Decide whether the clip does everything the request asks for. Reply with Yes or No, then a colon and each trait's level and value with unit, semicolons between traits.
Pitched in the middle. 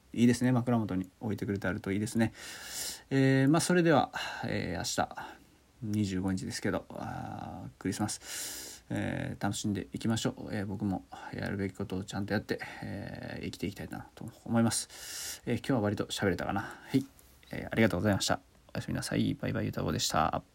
No: low, 105 Hz